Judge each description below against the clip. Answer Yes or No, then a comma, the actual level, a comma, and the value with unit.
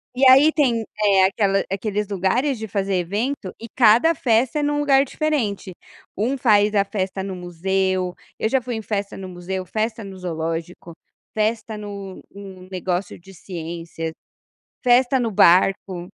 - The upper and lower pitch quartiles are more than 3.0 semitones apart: Yes, average, 3.7 semitones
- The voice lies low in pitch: No, high, 200 Hz